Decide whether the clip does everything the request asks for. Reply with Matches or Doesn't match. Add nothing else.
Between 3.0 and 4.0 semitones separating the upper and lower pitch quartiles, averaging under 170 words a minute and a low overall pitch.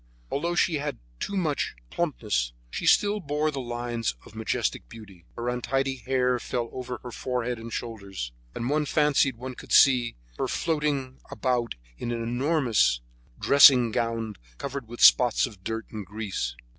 Matches